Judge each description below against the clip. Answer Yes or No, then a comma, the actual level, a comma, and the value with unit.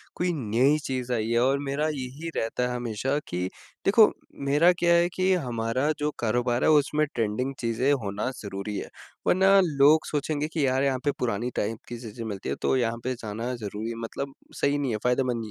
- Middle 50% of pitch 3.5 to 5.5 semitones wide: Yes, average, 4.1 semitones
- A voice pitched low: Yes, low, 125 Hz